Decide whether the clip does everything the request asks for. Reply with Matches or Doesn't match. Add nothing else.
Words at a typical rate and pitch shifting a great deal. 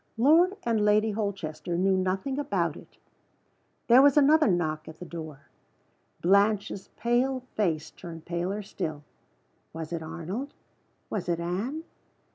Doesn't match